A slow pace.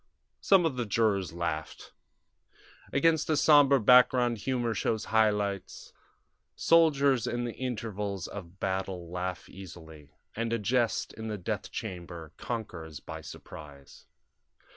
Yes: slow, 125 wpm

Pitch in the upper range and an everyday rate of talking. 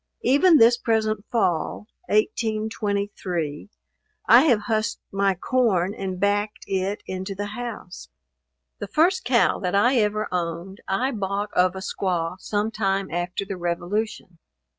No: high, 205 Hz; slow, 130 wpm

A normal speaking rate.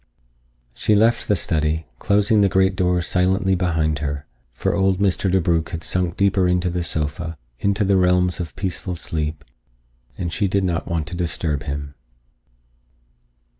Yes: average, 155 wpm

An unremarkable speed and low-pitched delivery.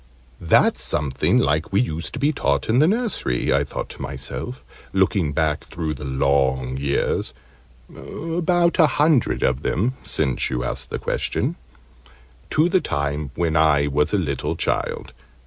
Yes: average, 160 wpm; very low, 75 Hz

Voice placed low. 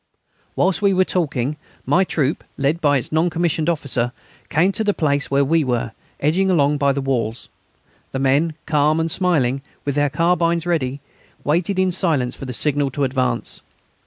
No: medium, 150 Hz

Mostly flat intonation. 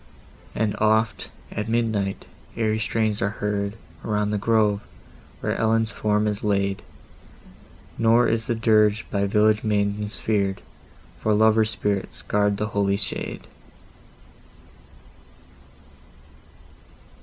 Yes: narrow, 1.4 semitones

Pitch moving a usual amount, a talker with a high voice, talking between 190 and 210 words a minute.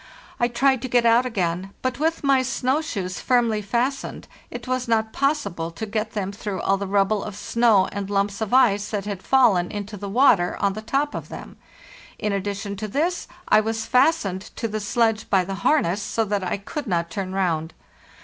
Yes: average, 4.0 semitones; high, 215 Hz; average, 200 wpm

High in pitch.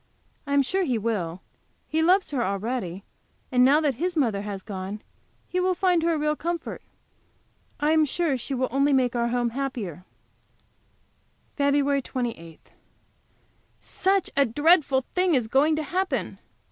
Yes: very high, 275 Hz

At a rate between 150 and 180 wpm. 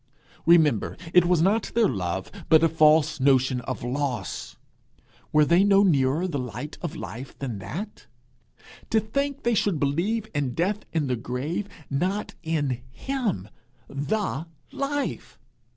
No: average, 140 wpm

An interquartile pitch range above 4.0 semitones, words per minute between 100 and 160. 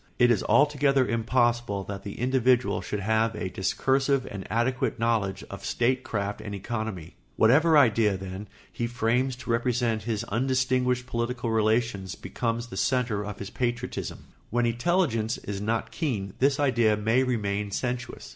No: average, 3.3 semitones; average, 145 wpm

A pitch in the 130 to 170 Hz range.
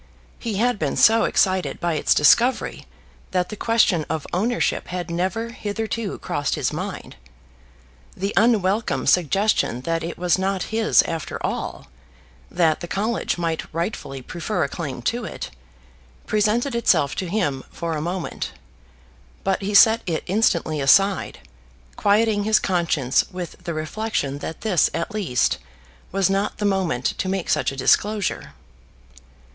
No: medium, 185 Hz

